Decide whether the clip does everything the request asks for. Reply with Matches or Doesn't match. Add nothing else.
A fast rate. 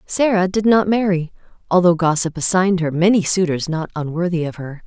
Doesn't match